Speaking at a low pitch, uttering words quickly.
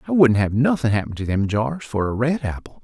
Yes: low, 120 Hz; fast, 255 wpm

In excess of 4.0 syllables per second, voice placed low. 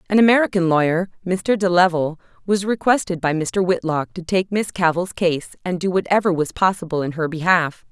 No: 5.4 syllables/s; medium, 180 Hz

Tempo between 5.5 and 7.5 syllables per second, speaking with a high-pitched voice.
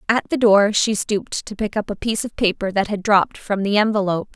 Yes: 6.1 syllables/s; high, 205 Hz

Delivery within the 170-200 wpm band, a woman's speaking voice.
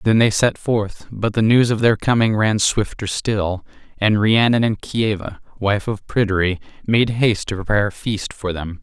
No: average, 190 wpm; male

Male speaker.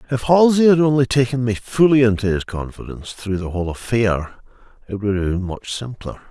Yes: male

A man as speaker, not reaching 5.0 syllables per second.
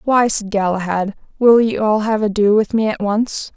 No: female; 4.7 syllables/s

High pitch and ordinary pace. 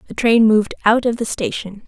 No: high, 225 Hz; fast, 225 wpm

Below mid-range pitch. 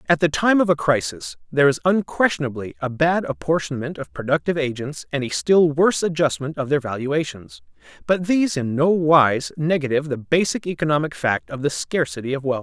No: medium, 150 Hz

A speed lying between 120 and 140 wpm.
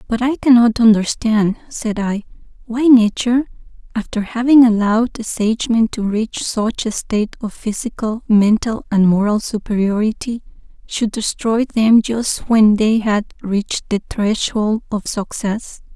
Yes: slow, 135 wpm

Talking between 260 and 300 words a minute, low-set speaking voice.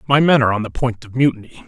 Yes: fast, 285 wpm; low, 125 Hz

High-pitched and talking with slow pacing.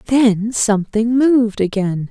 Yes: high, 225 Hz; slow, 115 wpm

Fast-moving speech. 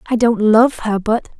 Yes: fast, 215 wpm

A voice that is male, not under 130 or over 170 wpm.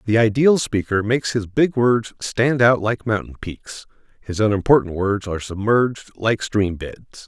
Yes: male; average, 165 wpm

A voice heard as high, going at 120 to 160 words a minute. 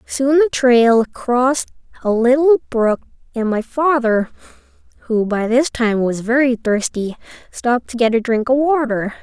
Yes: high, 245 Hz; average, 155 wpm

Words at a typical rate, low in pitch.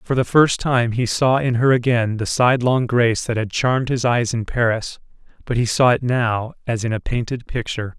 No: fast, 220 wpm; low, 120 Hz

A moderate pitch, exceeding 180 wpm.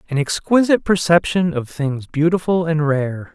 No: medium, 160 Hz; average, 145 wpm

